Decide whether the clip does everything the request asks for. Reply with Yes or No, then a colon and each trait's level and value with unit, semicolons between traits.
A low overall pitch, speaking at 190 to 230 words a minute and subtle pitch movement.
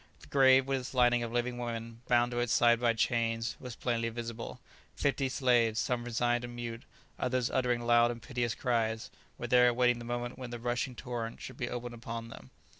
Yes: low, 120 Hz; average, 200 wpm; narrow, 1.0 semitones